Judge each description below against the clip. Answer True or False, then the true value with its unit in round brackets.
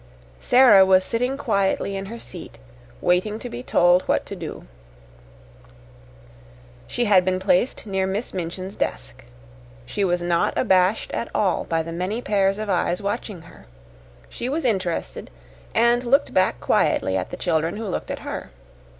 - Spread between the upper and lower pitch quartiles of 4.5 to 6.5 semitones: False (4.0 semitones)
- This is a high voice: True (195 Hz)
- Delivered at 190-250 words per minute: False (160 wpm)